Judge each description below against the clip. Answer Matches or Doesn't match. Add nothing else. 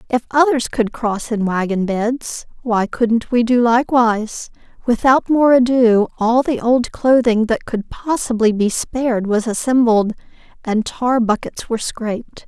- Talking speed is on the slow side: Doesn't match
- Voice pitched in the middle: Doesn't match